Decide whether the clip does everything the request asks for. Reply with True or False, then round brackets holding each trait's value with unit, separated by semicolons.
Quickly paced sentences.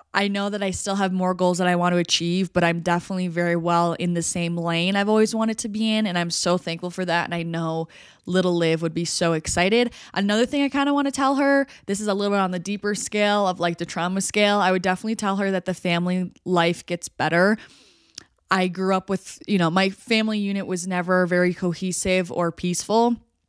True (235 wpm)